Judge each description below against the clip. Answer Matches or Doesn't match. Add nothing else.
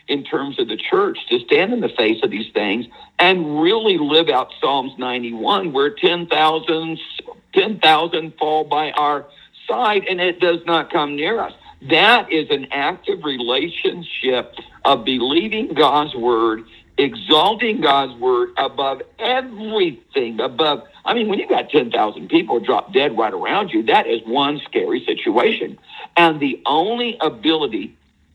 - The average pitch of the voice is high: Matches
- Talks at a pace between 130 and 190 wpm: Matches